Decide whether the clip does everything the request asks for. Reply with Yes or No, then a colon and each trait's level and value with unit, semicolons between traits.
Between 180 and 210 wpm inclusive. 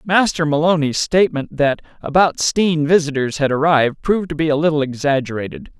No: average, 155 wpm